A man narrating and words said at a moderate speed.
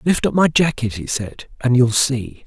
No: male; fast, 220 wpm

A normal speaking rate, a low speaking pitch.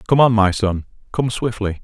Yes: average, 195 wpm; low, 105 Hz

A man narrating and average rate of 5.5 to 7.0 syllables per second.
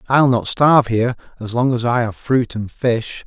No: male; 4.9 syllables/s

